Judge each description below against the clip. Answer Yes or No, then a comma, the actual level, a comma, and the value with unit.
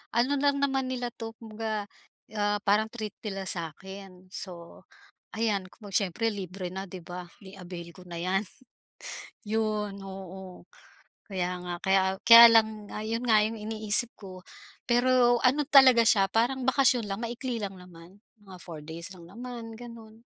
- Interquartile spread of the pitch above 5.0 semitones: No, average, 3.8 semitones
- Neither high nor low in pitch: No, high, 210 Hz